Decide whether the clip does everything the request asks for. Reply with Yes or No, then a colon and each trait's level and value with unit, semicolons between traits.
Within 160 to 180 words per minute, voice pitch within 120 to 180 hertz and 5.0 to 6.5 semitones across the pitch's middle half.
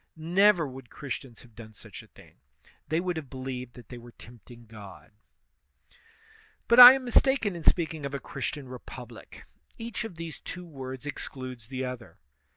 Yes: average, 170 wpm; low, 135 Hz; wide, 5.6 semitones